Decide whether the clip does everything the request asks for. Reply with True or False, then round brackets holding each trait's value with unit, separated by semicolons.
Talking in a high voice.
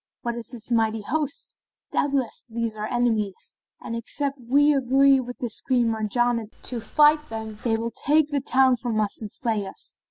True (240 Hz)